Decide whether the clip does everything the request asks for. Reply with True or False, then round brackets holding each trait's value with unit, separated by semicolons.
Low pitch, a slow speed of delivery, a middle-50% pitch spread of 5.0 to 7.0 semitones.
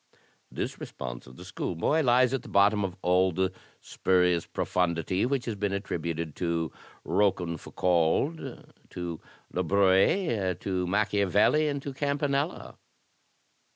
True (95 Hz; 120 wpm; 5.6 semitones)